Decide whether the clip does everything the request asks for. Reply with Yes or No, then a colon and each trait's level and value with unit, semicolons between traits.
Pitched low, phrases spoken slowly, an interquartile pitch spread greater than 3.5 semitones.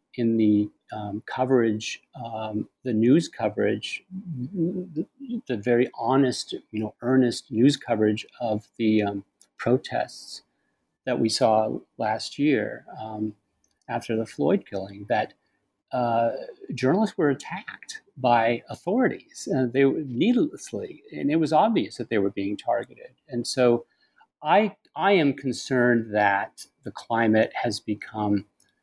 Yes: low, 115 Hz; slow, 130 wpm; average, 4.0 semitones